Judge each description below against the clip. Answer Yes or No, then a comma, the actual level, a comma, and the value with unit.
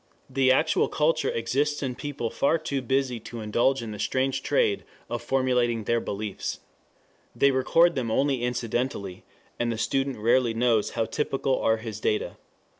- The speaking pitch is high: No, low, 125 Hz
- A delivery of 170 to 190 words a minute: No, average, 160 wpm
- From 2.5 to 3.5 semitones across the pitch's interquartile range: Yes, average, 2.9 semitones